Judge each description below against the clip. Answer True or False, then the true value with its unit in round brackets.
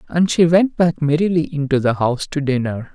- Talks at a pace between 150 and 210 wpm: True (205 wpm)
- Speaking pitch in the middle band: True (155 Hz)